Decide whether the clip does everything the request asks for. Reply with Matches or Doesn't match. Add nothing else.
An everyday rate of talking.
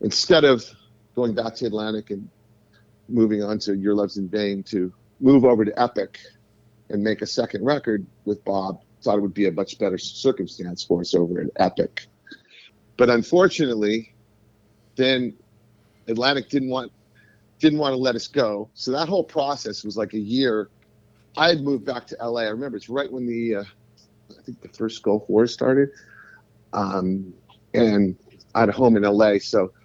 Matches